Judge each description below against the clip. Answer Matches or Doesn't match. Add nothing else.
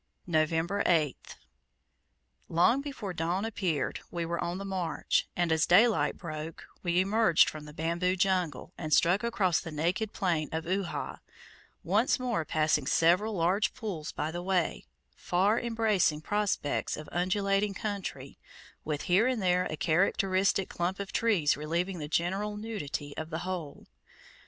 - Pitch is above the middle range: Doesn't match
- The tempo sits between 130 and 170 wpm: Matches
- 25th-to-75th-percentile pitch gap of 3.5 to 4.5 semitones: Matches